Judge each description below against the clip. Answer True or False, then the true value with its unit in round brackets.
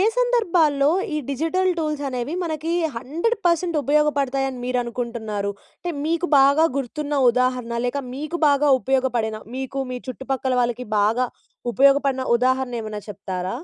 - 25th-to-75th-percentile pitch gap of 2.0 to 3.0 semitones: False (3.7 semitones)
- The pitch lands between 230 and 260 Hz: False (270 Hz)